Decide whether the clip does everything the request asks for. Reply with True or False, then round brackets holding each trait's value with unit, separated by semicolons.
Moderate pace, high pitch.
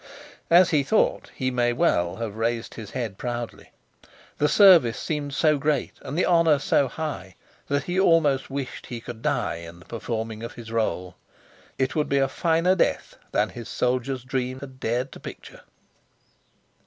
False (170 wpm; 130 Hz)